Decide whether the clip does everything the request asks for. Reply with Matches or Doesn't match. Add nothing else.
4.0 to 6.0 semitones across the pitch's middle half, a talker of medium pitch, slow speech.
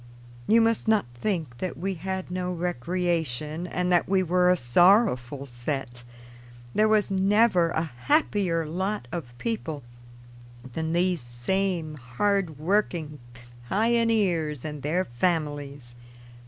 Matches